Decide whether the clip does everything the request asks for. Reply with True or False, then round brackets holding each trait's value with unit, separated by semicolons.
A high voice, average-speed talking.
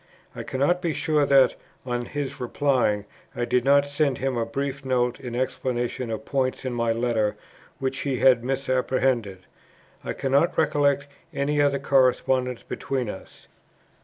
False (130 Hz; 150 wpm)